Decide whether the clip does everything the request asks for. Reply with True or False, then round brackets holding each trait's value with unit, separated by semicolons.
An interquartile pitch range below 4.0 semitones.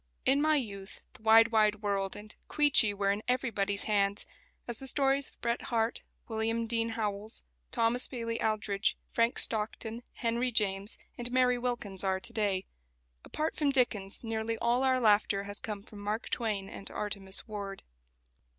True (2.9 semitones)